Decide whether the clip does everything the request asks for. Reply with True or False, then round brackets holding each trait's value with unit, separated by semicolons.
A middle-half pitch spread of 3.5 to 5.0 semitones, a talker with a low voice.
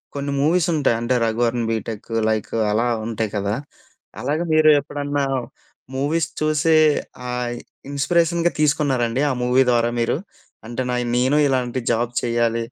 True (3.9 semitones; 125 Hz)